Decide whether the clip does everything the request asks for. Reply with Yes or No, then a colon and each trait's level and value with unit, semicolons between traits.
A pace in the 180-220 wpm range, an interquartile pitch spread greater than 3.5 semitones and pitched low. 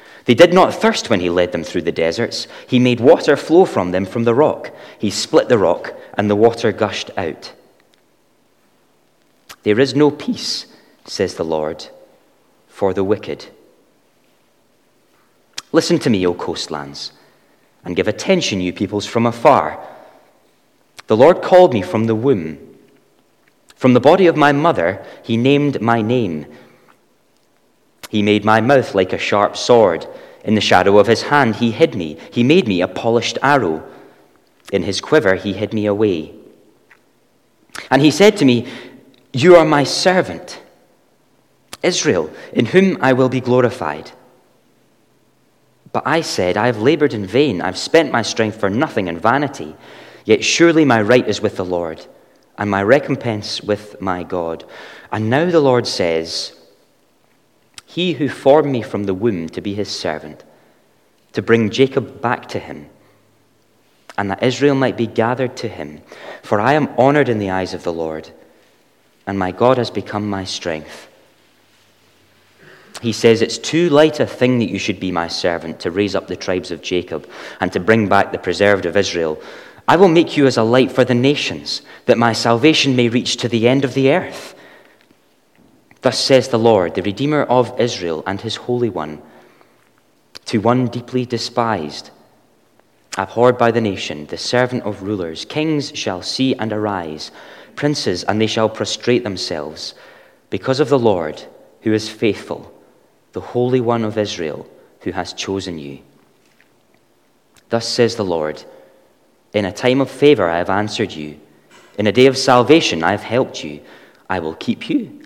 No: average, 165 wpm; average, 5.1 semitones; low, 115 Hz